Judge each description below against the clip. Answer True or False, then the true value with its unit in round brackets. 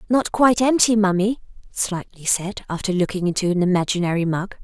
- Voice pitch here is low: False (195 Hz)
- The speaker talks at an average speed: True (155 wpm)